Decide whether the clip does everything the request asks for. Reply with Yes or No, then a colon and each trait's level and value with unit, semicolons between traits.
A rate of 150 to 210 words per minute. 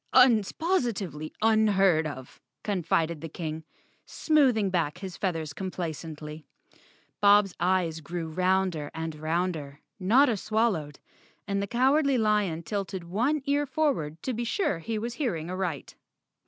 No: average, 140 wpm